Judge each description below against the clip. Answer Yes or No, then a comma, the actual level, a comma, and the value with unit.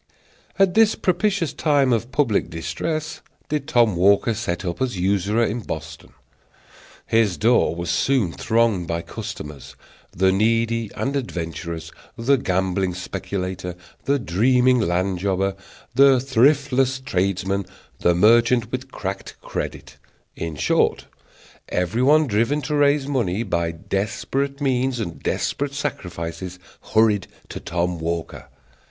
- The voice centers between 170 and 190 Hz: No, low, 110 Hz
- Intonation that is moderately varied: No, wide, 6.6 semitones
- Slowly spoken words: Yes, slow, 120 wpm